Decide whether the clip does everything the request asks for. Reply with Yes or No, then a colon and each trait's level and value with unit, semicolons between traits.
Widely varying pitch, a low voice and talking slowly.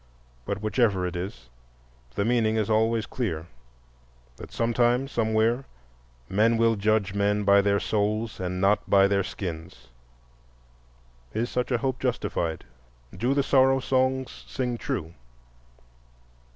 No: average, 3.5 semitones; low, 110 Hz; slow, 125 wpm